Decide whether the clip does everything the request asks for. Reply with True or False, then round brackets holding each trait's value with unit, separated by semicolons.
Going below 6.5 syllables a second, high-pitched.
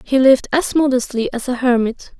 True (5.5 syllables/s; 260 Hz)